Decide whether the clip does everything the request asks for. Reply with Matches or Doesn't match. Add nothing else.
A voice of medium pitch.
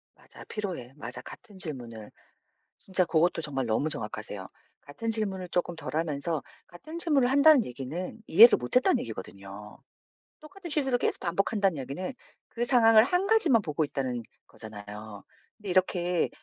Matches